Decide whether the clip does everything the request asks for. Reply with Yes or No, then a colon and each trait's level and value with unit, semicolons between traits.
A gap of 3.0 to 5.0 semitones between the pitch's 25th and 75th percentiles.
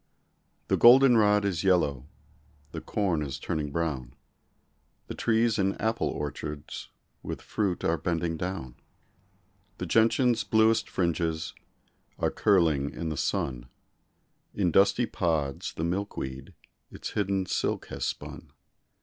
No: wide, 5.5 semitones